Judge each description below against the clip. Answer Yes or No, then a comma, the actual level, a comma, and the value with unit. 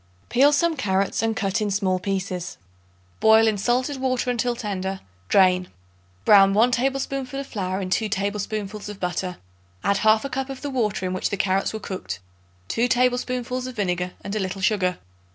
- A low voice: No, high, 210 Hz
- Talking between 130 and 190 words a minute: Yes, average, 175 wpm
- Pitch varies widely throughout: No, average, 4.6 semitones